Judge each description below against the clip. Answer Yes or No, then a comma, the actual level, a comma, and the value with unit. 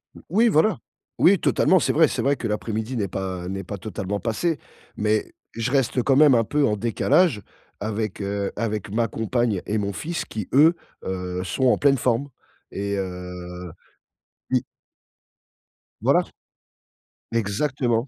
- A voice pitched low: Yes, low, 110 Hz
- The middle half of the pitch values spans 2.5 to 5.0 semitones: No, wide, 5.5 semitones